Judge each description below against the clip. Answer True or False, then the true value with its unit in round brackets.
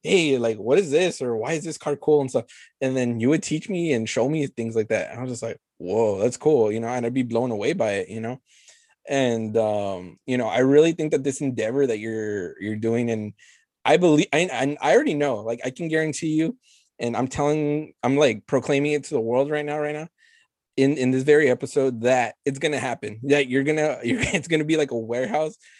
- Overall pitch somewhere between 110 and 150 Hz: True (135 Hz)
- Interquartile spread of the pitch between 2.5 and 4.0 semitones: False (4.4 semitones)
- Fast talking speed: True (245 wpm)